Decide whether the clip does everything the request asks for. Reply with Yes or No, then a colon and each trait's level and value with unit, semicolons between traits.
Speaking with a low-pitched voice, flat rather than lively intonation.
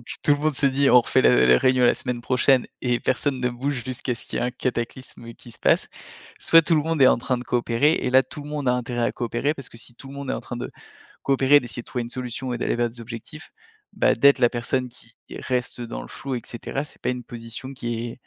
Yes: low, 125 Hz; narrow, 2.3 semitones